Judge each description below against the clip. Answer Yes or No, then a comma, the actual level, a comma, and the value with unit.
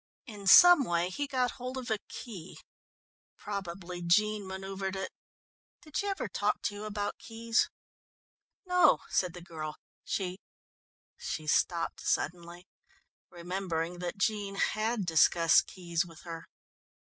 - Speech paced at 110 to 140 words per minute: Yes, slow, 135 wpm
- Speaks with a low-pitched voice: No, high, 190 Hz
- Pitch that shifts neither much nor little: Yes, average, 4.0 semitones